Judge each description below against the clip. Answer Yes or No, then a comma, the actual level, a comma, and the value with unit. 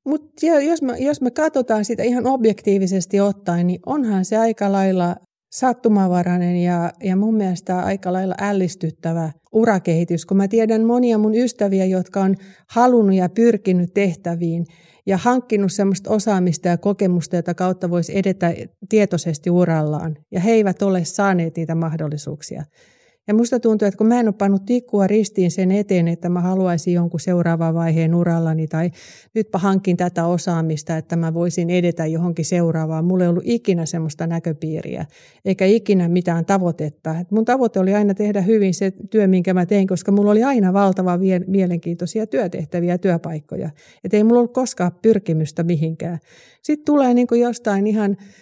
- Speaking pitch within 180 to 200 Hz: Yes, high, 190 Hz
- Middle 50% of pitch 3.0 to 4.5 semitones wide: Yes, average, 3.7 semitones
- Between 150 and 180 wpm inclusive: Yes, fast, 155 wpm